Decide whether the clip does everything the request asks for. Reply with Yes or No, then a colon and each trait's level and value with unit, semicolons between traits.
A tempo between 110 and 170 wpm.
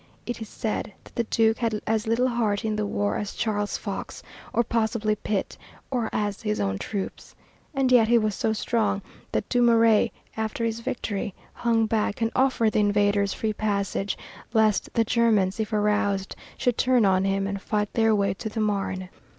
No: average, 185 wpm